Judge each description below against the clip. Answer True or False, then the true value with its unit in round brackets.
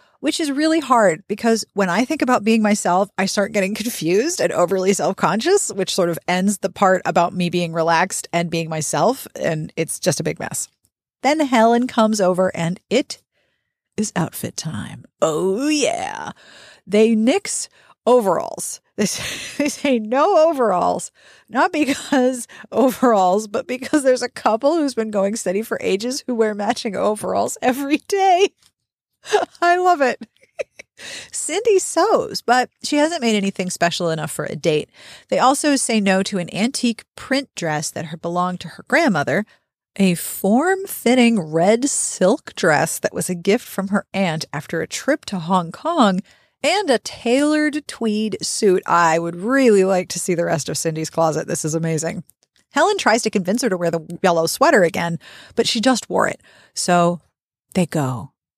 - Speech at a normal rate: True (170 wpm)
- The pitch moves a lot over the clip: True (6.7 semitones)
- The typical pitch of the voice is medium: False (210 Hz)